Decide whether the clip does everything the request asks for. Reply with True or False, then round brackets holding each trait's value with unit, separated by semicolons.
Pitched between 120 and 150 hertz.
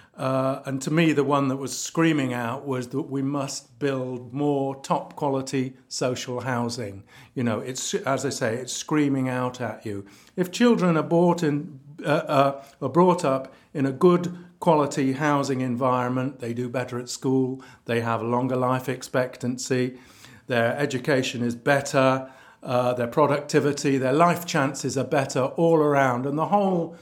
True (135 Hz)